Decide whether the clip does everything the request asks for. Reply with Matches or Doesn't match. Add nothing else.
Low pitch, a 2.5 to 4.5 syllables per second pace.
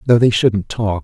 Matches